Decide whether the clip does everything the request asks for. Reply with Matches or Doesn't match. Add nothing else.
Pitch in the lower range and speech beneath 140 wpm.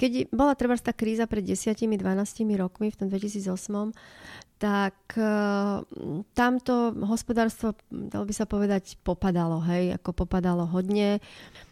Doesn't match